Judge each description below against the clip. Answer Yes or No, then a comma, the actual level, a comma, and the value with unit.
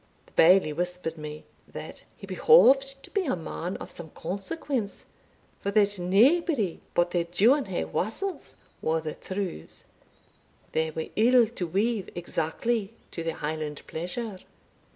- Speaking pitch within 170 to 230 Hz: Yes, high, 190 Hz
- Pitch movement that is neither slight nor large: No, wide, 6.4 semitones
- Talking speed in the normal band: No, slow, 130 wpm